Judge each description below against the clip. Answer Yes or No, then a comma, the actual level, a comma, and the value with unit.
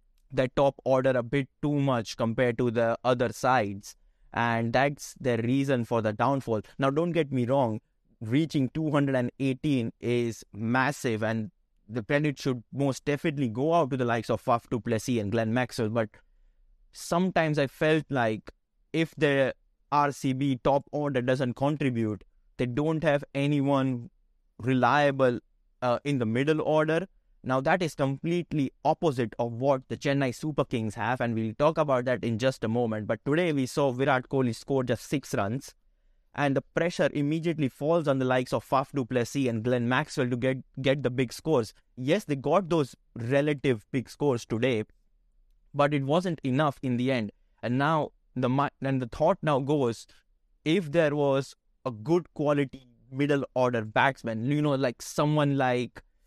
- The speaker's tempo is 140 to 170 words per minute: Yes, average, 165 wpm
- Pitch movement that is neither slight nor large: Yes, average, 3.3 semitones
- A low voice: Yes, low, 130 Hz